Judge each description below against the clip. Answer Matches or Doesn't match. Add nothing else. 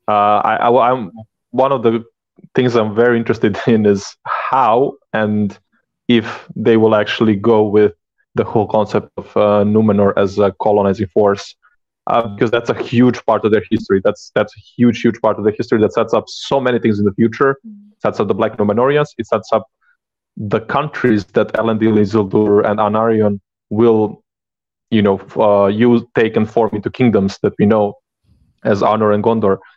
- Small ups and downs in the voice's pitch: Matches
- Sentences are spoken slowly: Doesn't match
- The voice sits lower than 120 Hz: Matches